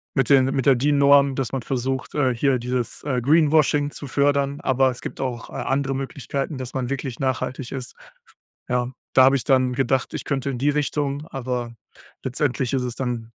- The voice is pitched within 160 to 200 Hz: No, low, 135 Hz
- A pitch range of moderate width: No, narrow, 1.9 semitones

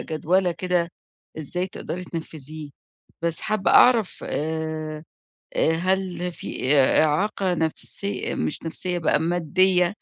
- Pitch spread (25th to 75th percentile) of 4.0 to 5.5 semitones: No, average, 2.7 semitones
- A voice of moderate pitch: Yes, medium, 170 Hz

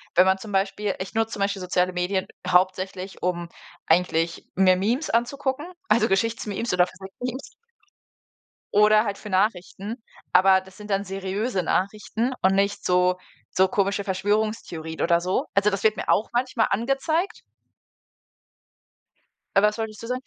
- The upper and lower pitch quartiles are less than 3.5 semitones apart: Yes, average, 2.9 semitones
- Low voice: No, high, 200 Hz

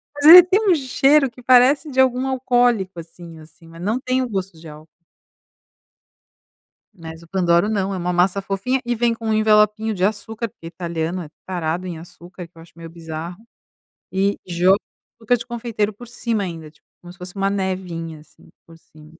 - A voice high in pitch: Yes, high, 195 Hz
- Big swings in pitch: Yes, wide, 5.8 semitones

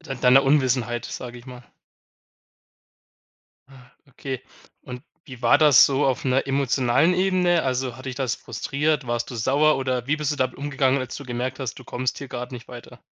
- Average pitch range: No, narrow, 2.2 semitones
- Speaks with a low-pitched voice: Yes, low, 130 Hz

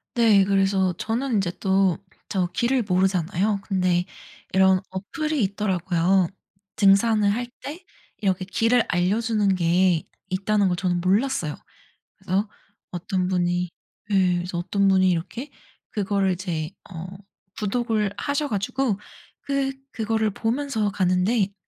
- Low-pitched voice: No, high, 195 Hz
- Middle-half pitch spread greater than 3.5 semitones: No, average, 3.2 semitones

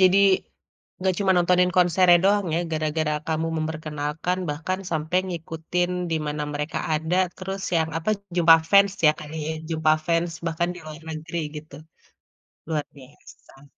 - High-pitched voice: No, medium, 160 Hz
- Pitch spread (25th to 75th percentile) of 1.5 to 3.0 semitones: Yes, narrow, 2.6 semitones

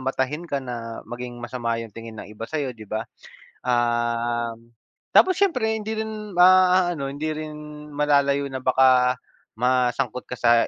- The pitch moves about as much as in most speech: Yes, average, 4.7 semitones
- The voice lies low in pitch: Yes, low, 130 Hz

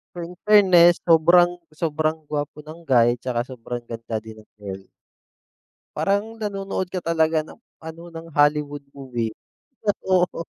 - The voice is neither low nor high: Yes, medium, 160 Hz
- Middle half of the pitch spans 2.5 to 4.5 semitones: No, wide, 5.6 semitones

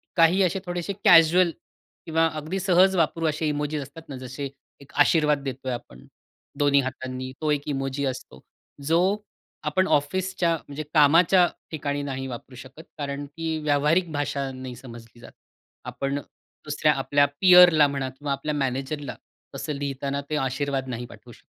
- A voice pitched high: No, medium, 145 Hz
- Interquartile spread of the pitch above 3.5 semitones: No, average, 3.2 semitones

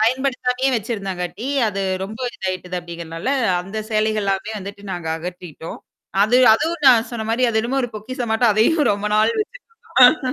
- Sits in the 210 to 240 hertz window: Yes, high, 215 Hz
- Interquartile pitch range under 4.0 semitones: No, average, 4.5 semitones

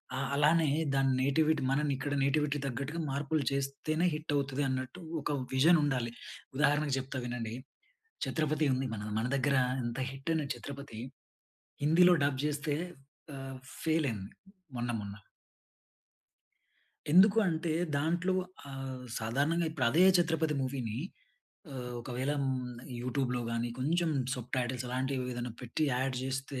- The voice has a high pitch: No, low, 135 Hz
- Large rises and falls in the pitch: No, average, 3.2 semitones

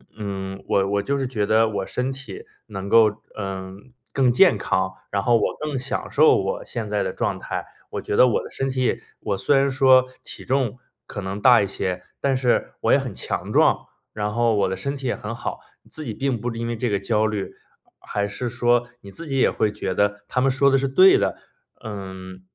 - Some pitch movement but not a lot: Yes, average, 4.9 semitones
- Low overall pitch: Yes, low, 115 Hz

